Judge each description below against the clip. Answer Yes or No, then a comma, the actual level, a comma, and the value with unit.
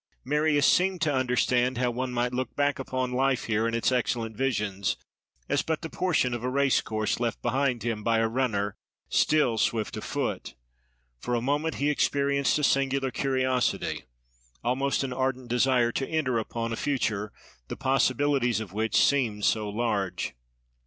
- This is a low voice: Yes, low, 125 Hz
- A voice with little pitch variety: No, average, 3.0 semitones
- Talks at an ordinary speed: Yes, average, 165 wpm